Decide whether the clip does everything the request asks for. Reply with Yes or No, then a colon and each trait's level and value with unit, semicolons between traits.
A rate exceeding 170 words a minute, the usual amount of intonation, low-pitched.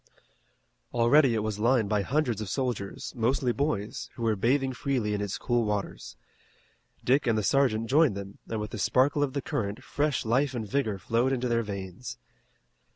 Yes: average, 180 wpm; average, 4.0 semitones; low, 115 Hz